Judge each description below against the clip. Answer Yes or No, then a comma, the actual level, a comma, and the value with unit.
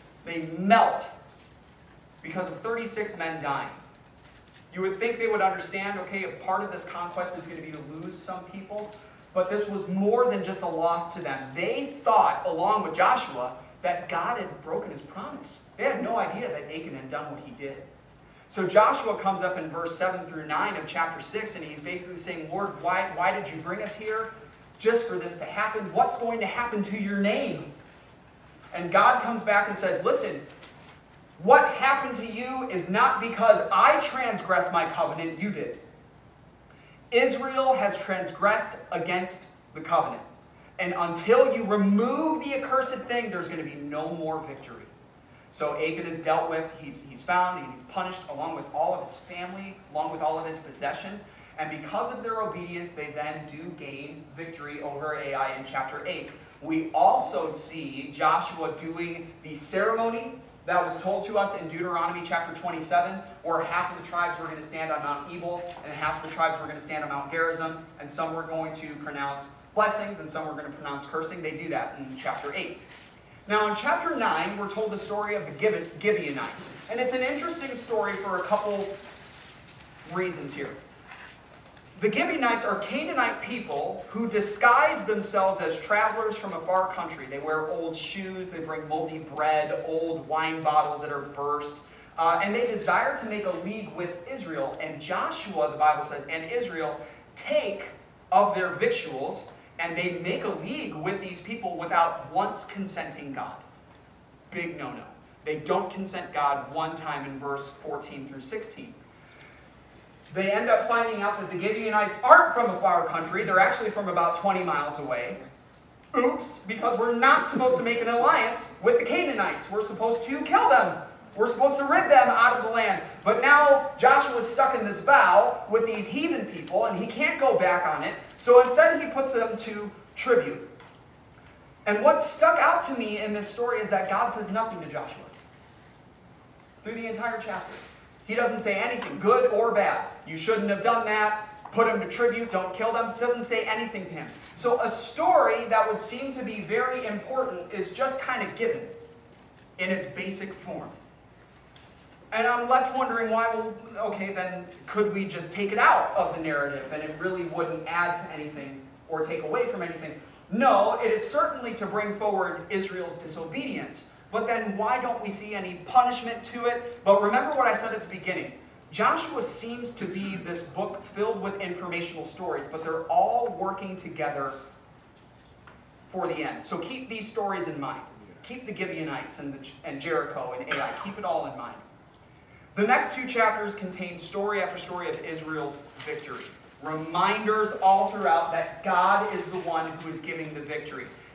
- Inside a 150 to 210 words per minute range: Yes, average, 180 wpm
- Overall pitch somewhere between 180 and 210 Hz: Yes, high, 190 Hz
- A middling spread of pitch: No, wide, 5.9 semitones